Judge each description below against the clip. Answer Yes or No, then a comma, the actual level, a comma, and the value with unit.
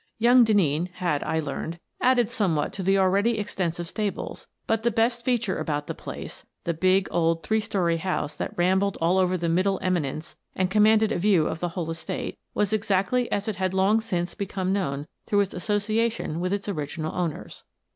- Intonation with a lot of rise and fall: No, average, 3.8 semitones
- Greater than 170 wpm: Yes, average, 195 wpm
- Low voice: No, high, 190 Hz